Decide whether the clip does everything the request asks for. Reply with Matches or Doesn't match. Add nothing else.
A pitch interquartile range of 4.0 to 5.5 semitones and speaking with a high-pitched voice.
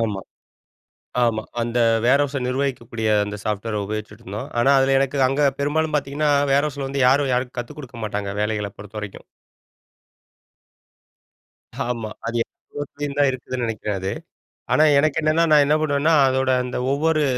Doesn't match